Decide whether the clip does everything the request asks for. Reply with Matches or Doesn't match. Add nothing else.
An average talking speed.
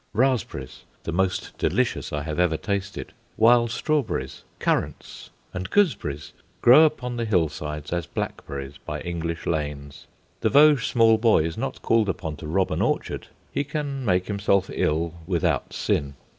Matches